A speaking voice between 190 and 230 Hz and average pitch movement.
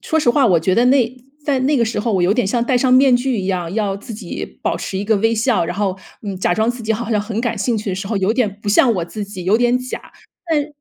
Yes: high, 220 Hz; average, 3.9 semitones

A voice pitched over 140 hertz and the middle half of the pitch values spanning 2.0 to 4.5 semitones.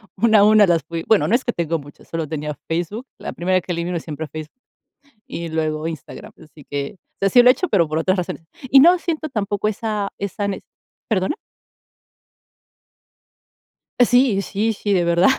No: medium, 185 Hz; average, 5.0 semitones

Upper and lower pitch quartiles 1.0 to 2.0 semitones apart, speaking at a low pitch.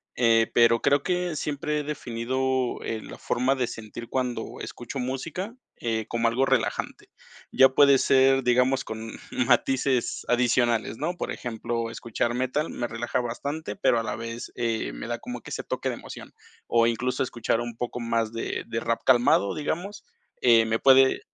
No: narrow, 2.5 semitones; low, 120 Hz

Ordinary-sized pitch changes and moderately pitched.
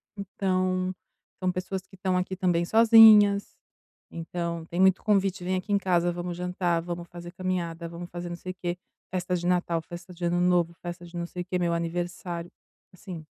No: narrow, 1.2 semitones; medium, 180 Hz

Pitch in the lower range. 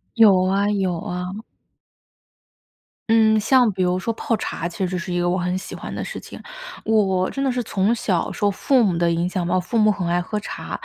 No: high, 190 Hz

